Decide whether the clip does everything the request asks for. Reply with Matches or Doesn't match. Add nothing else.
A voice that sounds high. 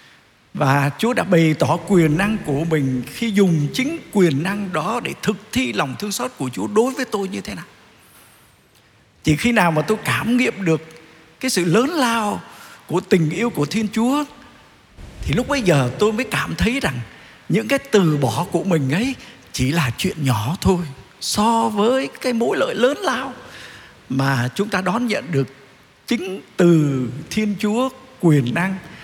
Doesn't match